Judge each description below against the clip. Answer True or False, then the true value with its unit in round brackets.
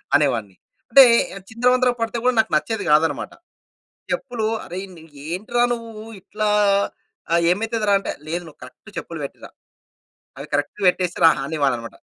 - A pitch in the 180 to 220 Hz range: True (195 Hz)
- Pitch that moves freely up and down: True (6.8 semitones)